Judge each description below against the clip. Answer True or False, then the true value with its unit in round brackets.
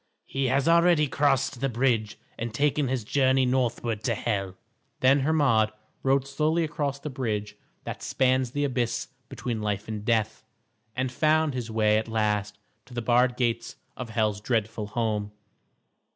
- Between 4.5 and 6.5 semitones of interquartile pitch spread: False (3.8 semitones)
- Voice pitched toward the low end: True (125 Hz)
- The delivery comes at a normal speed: True (155 wpm)